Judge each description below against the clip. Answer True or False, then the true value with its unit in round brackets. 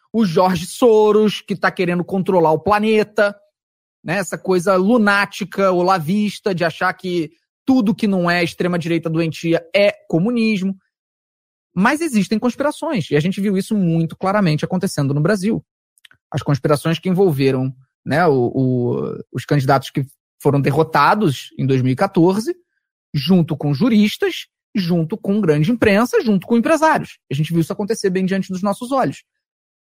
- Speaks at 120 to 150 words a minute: True (145 wpm)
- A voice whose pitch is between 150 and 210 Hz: True (190 Hz)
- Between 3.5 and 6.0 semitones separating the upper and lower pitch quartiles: True (4.5 semitones)